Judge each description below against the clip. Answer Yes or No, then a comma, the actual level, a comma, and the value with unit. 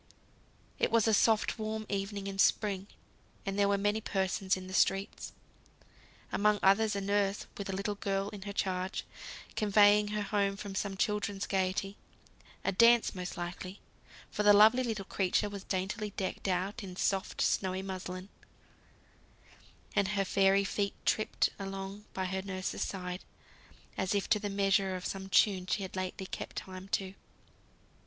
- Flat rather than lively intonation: Yes, narrow, 1.4 semitones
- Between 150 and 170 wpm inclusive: Yes, average, 160 wpm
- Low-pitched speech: No, high, 195 Hz